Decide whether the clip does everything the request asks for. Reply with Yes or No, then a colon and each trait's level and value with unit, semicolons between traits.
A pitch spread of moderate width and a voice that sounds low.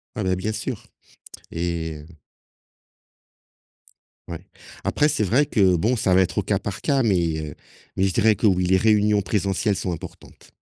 Yes: average, 3.2 semitones; very low, 95 Hz